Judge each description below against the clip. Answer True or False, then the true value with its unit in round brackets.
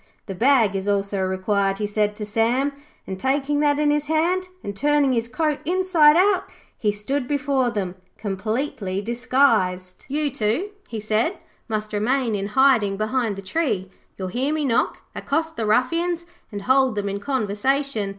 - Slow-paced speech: False (170 wpm)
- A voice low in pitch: False (240 Hz)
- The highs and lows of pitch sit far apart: True (5.9 semitones)